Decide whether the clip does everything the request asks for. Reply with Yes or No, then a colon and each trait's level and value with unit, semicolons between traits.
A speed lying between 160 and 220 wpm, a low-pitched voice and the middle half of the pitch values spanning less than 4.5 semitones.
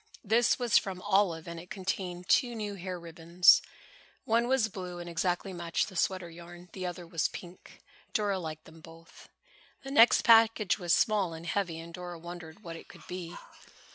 No: average, 180 wpm; medium, 180 Hz; average, 3.1 semitones